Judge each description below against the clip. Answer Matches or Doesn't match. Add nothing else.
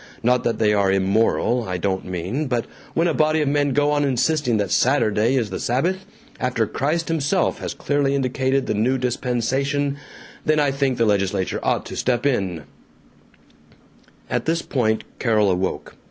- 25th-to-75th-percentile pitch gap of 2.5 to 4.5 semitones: Doesn't match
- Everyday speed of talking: Matches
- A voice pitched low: Matches